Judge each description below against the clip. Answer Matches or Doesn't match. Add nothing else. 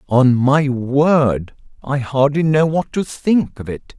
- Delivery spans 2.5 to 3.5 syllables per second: Matches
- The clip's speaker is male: Matches